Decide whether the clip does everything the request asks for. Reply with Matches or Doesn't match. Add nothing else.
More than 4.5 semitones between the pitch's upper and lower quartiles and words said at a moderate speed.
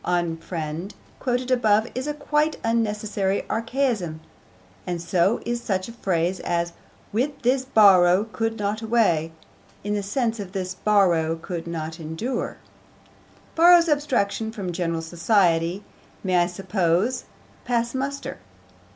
Doesn't match